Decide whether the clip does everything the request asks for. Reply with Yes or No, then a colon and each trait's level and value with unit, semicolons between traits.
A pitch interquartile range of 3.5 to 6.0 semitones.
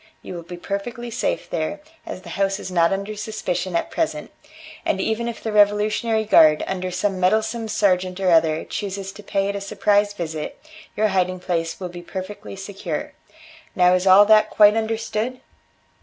No: average, 2.8 semitones